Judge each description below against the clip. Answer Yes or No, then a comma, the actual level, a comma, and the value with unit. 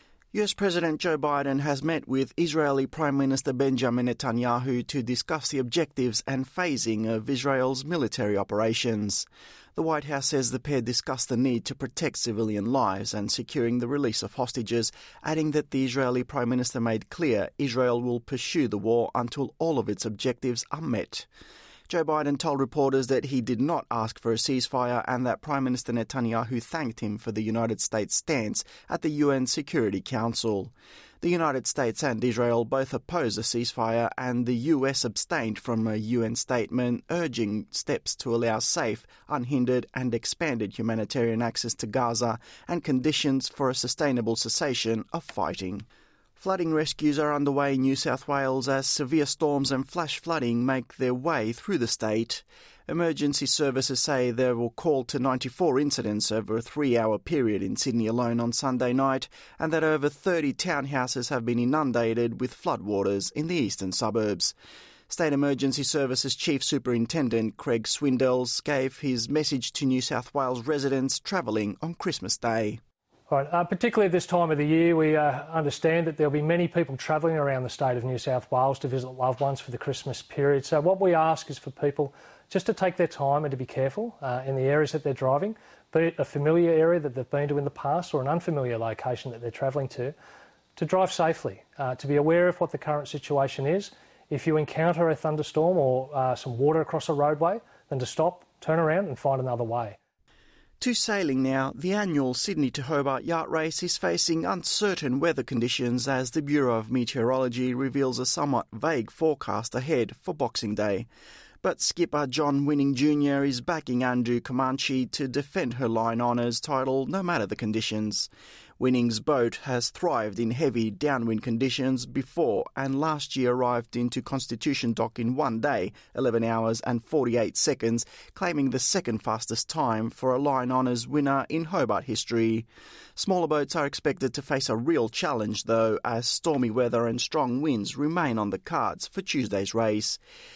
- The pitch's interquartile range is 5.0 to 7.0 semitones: No, average, 4.0 semitones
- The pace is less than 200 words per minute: Yes, average, 180 wpm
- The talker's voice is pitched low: Yes, low, 130 Hz